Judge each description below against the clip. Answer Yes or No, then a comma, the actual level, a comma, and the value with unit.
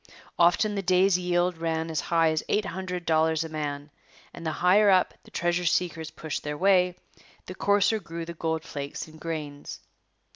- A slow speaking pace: No, average, 180 wpm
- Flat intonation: Yes, narrow, 2.3 semitones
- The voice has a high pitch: No, medium, 170 Hz